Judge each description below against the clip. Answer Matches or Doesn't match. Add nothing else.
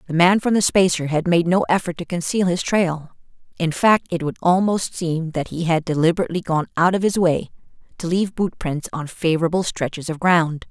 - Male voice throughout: Doesn't match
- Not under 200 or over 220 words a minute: Matches